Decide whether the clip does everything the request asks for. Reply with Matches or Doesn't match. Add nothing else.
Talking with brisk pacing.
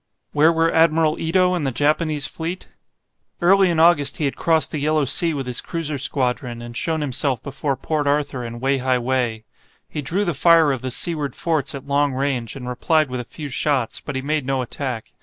Matches